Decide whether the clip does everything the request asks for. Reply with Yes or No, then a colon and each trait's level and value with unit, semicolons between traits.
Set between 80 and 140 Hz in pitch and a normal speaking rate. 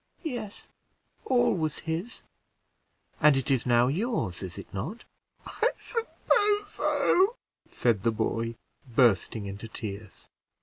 No: low, 135 Hz; slow, 120 wpm